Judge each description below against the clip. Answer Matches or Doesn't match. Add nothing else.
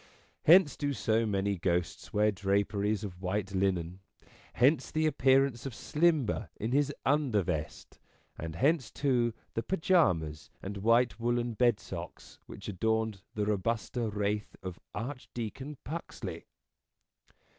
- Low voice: Matches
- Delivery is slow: Matches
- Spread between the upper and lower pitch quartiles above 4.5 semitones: Matches